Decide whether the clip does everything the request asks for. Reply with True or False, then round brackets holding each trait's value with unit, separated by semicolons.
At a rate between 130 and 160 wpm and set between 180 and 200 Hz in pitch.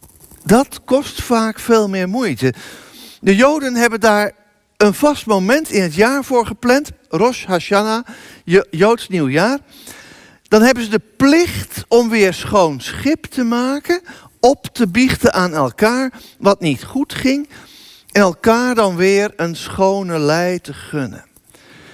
False (140 wpm; 220 Hz)